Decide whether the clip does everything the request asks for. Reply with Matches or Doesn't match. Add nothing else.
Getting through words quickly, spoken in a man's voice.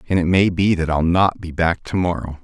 Matches